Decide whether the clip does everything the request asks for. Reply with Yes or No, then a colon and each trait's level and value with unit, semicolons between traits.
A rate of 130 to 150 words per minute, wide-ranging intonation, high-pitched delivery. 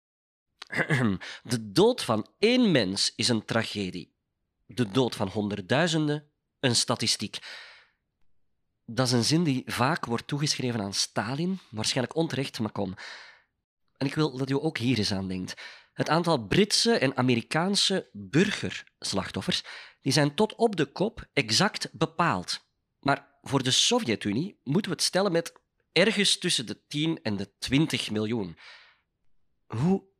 No: average, 140 wpm; wide, 6.8 semitones; low, 130 Hz